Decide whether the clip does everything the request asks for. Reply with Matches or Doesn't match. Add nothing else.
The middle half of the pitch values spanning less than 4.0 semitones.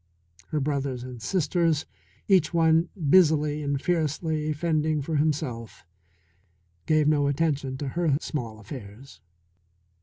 Matches